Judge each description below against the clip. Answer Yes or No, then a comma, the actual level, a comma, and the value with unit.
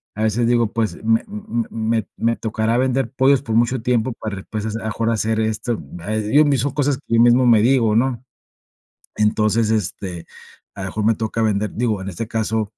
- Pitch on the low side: Yes, low, 115 Hz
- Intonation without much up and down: Yes, narrow, 2.1 semitones